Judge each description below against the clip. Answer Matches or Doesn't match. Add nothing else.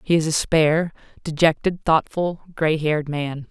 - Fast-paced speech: Doesn't match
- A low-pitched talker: Doesn't match